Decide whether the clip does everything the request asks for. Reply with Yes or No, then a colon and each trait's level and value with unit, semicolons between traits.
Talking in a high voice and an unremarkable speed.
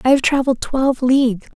Yes: very high, 260 Hz; average, 195 wpm